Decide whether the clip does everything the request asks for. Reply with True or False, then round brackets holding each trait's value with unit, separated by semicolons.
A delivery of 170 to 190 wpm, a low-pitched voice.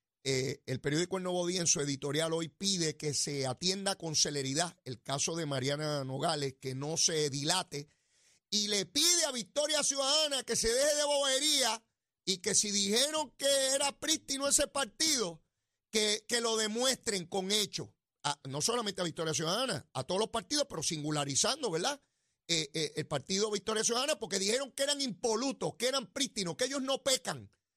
False (175 wpm; 195 Hz)